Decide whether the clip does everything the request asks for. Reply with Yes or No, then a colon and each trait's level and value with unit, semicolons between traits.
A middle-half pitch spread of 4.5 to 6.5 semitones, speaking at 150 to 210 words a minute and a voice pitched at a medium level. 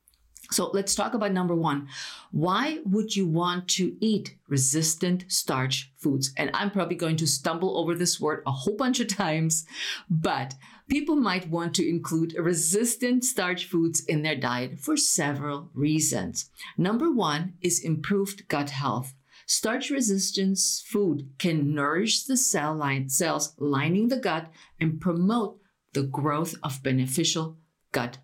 No: average, 5.0 semitones; average, 140 wpm; medium, 170 Hz